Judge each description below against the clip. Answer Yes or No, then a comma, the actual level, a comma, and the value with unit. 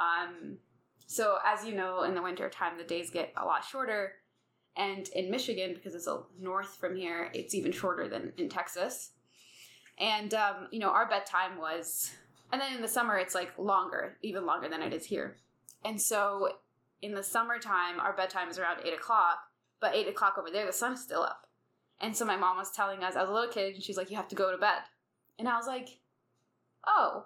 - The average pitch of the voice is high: Yes, high, 195 Hz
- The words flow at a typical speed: No, fast, 215 wpm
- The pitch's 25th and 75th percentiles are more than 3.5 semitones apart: No, average, 2.7 semitones